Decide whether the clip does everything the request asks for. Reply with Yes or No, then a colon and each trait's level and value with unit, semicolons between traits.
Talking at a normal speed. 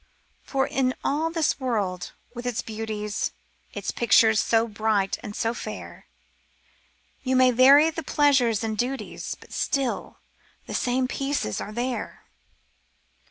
No: slow, 130 wpm